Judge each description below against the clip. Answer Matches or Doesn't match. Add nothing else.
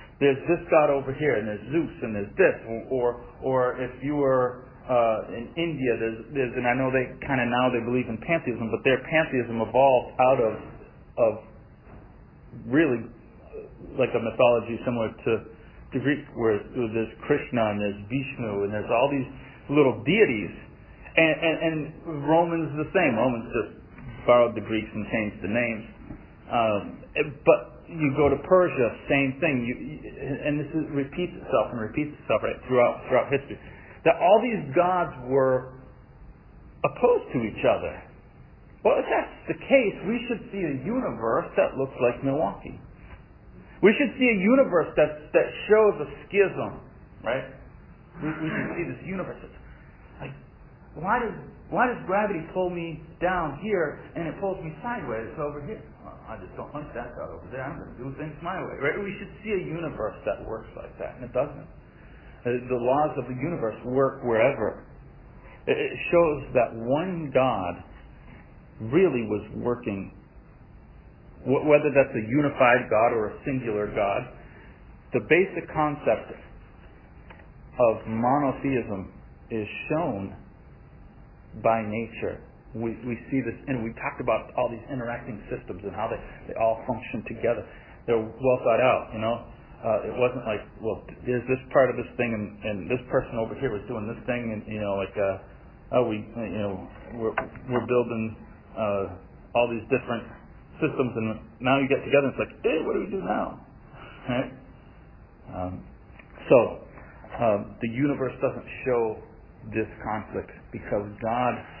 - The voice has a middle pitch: Doesn't match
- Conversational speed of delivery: Matches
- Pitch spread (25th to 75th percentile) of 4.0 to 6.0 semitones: Matches